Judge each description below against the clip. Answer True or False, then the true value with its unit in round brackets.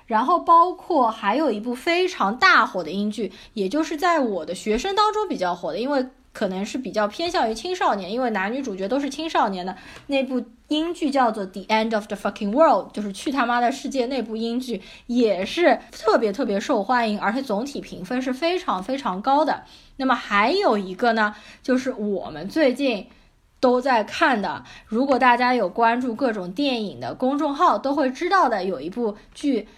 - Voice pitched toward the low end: False (245 Hz)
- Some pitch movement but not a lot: True (5.0 semitones)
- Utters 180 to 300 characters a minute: False (320 characters per minute)